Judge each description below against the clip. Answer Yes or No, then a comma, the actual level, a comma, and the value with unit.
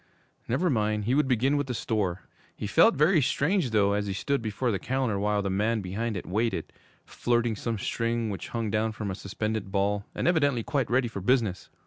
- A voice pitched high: No, low, 110 Hz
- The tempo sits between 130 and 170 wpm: No, fast, 205 wpm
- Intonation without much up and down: No, average, 3.7 semitones